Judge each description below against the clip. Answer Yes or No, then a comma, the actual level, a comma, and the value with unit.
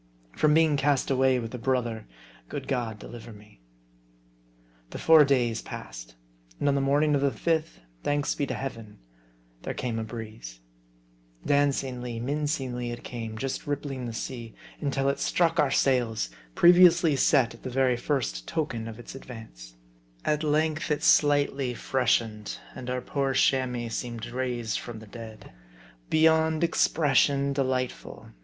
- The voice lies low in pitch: Yes, low, 130 Hz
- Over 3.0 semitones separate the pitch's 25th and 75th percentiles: Yes, average, 3.9 semitones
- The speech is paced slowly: No, average, 150 wpm